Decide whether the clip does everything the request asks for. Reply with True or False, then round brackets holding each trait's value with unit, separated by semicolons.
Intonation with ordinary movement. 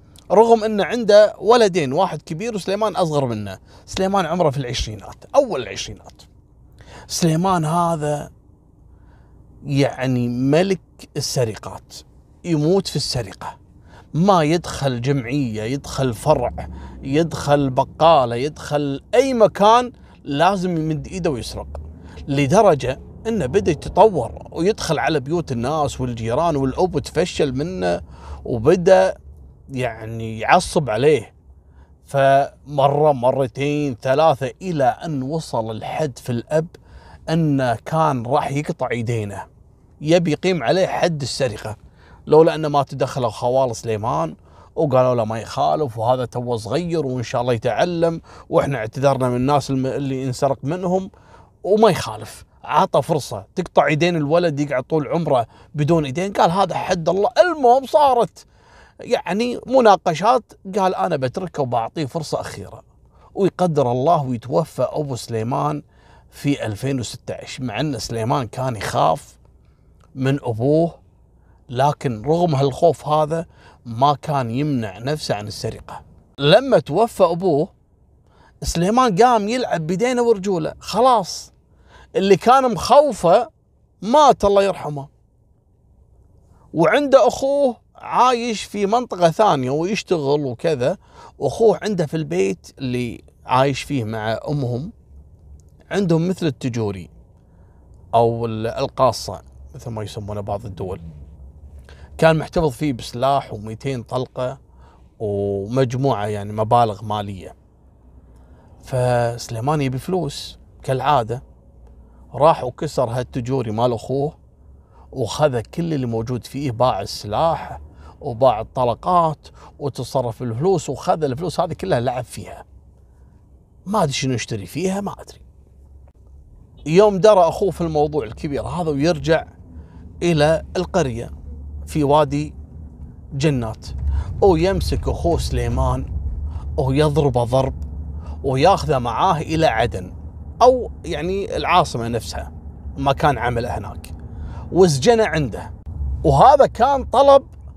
False (7.8 semitones)